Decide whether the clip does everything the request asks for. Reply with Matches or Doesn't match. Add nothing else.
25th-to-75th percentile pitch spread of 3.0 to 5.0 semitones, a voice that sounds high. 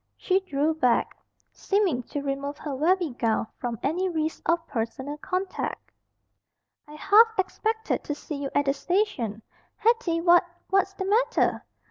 Doesn't match